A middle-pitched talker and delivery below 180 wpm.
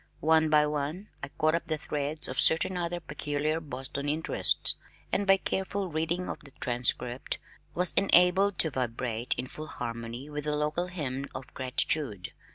Yes: medium, 150 Hz; average, 165 wpm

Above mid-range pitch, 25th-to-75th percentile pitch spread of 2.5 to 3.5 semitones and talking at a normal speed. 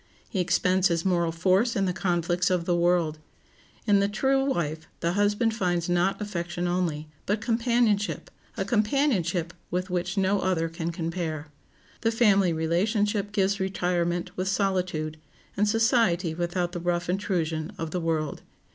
No: medium, 180 Hz; average, 3.0 semitones; average, 145 wpm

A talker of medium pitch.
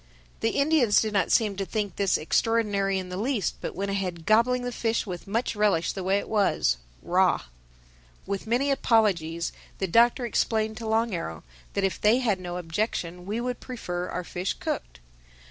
No: high, 205 Hz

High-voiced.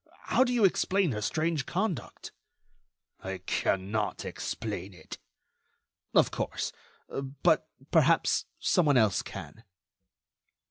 No: low, 120 Hz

